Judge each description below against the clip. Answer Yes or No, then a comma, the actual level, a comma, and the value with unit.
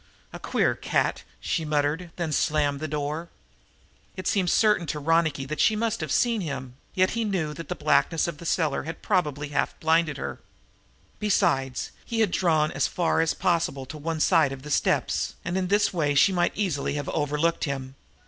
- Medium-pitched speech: Yes, medium, 160 Hz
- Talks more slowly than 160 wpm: No, average, 190 wpm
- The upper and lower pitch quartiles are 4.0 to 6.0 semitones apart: No, average, 3.6 semitones